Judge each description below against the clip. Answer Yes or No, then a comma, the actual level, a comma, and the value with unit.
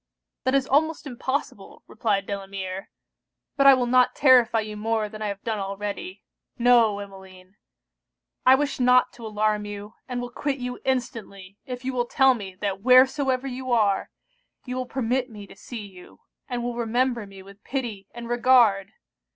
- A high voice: Yes, high, 235 Hz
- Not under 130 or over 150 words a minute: No, average, 170 wpm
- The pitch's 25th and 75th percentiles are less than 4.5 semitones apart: Yes, average, 4.0 semitones